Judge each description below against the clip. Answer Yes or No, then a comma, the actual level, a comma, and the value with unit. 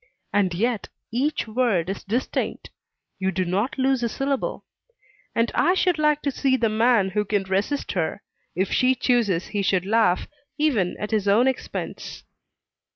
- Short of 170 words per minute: Yes, average, 160 wpm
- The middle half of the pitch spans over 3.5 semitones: Yes, average, 5.2 semitones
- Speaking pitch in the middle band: No, high, 225 Hz